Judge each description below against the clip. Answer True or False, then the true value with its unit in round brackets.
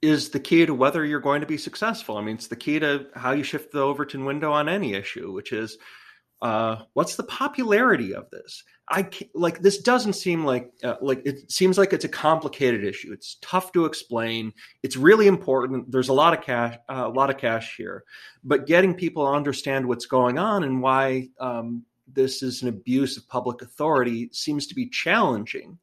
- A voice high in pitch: False (140 Hz)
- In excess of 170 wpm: True (205 wpm)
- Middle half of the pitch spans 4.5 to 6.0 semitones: True (5.2 semitones)